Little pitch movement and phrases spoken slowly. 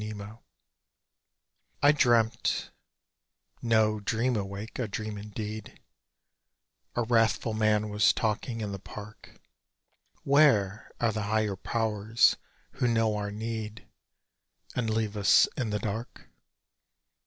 Yes: narrow, 1.6 semitones; slow, 110 wpm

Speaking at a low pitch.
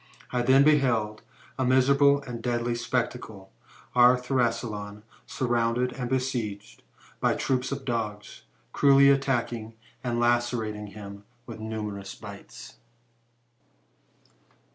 Yes: low, 120 Hz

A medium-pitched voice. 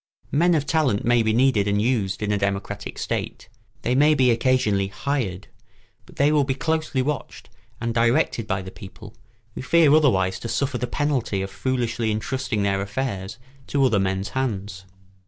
No: low, 115 Hz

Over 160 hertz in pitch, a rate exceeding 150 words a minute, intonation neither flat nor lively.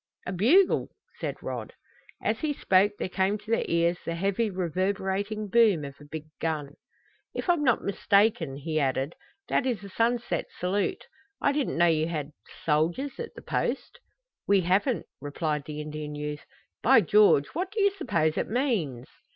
No: high, 190 Hz; average, 165 wpm; wide, 6.7 semitones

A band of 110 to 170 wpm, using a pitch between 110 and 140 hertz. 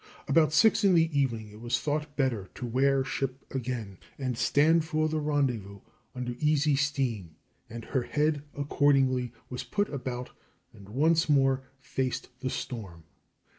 Yes: average, 150 wpm; low, 135 Hz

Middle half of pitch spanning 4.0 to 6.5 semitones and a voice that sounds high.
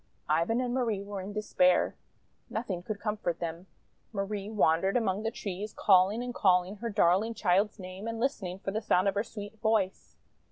No: average, 3.0 semitones; high, 205 Hz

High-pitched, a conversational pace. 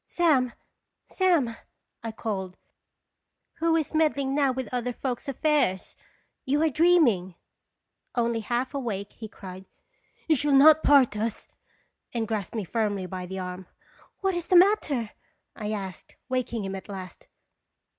Yes: high, 240 Hz; average, 160 wpm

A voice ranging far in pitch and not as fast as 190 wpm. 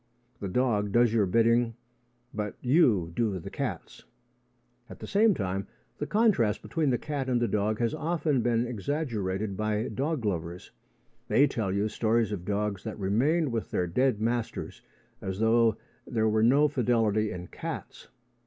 No: average, 3.7 semitones; average, 160 wpm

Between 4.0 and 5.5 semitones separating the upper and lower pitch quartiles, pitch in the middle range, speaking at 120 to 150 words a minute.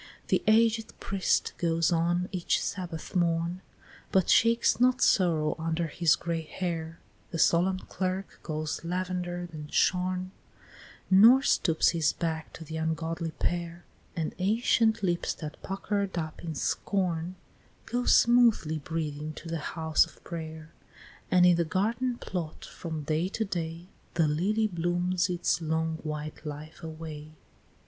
No: narrow, 2.6 semitones; medium, 170 Hz; average, 140 wpm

